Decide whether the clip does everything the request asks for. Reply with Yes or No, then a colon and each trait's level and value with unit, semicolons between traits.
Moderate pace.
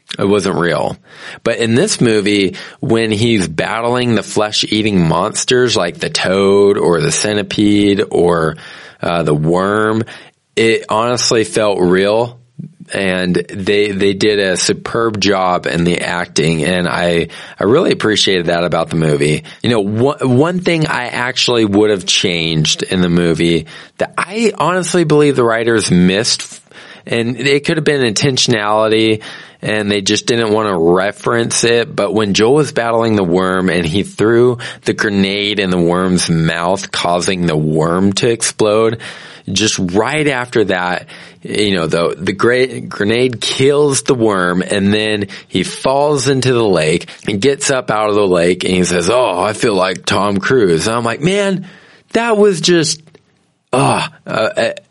Yes: average, 160 wpm